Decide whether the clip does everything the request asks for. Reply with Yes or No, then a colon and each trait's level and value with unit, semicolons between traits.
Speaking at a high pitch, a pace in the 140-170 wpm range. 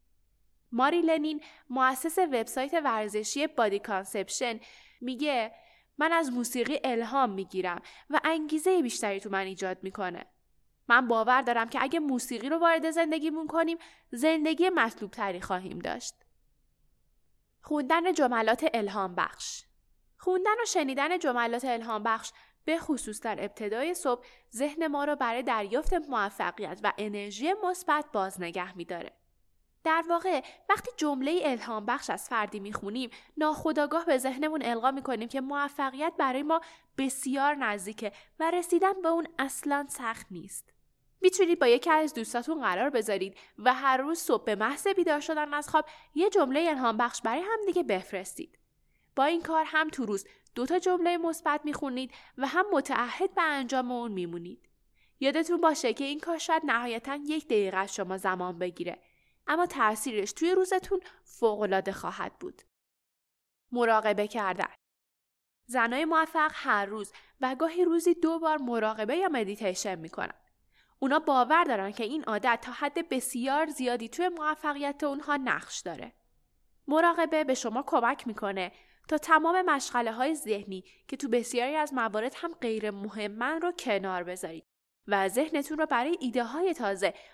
Yes: very high, 265 Hz; average, 145 wpm